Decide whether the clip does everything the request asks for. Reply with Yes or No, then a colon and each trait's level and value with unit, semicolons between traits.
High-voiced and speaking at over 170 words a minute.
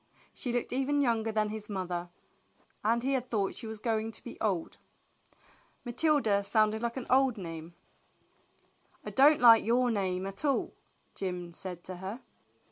No: high, 220 Hz; average, 160 wpm